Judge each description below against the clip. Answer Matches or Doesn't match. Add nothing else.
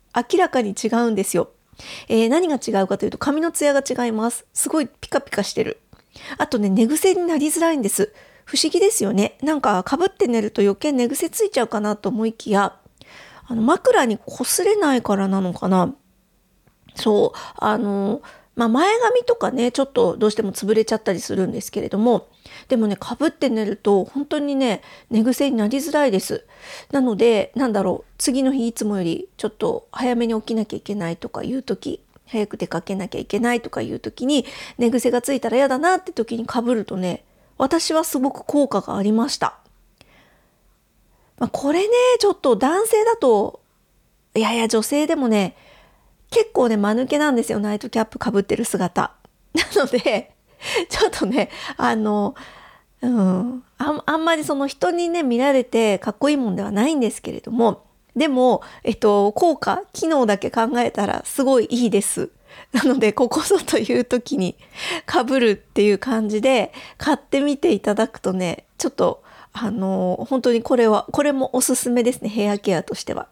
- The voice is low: Doesn't match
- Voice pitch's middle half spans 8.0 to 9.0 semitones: Doesn't match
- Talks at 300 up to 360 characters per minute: Matches